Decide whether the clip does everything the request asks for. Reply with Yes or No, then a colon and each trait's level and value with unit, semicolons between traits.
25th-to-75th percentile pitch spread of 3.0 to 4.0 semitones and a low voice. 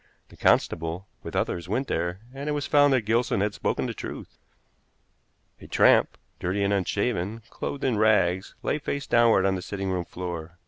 No: average, 5.0 semitones; low, 100 Hz